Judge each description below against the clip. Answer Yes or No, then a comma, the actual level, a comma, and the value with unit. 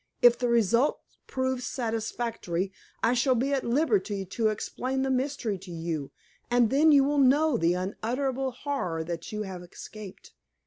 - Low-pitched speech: No, high, 235 Hz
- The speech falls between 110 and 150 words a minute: No, average, 160 wpm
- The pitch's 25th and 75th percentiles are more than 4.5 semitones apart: Yes, wide, 5.5 semitones